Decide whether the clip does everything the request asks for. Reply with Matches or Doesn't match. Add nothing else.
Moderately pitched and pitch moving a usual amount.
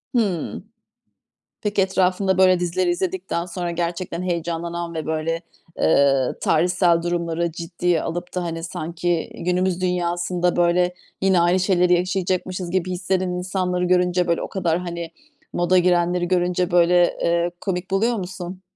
Doesn't match